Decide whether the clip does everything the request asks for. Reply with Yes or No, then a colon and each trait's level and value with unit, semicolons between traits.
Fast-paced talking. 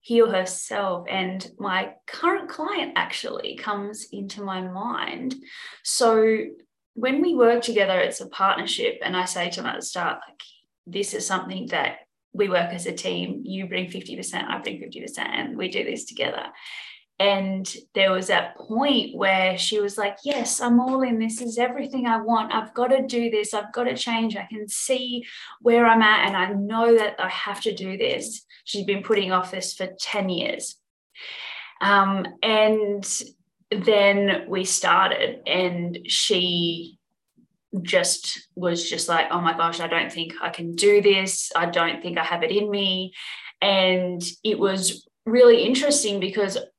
No: average, 175 wpm